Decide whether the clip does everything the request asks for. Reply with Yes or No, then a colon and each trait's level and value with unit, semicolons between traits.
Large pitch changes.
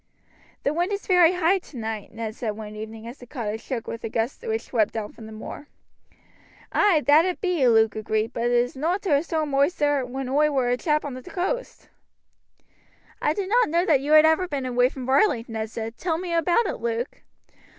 Yes: wide, 6.6 semitones